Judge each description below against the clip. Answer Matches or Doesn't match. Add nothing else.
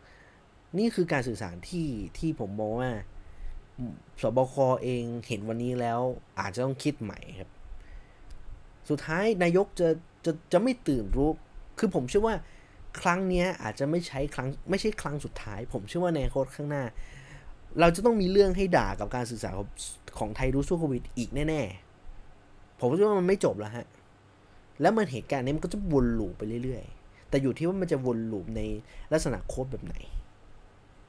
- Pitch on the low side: Matches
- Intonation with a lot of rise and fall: Matches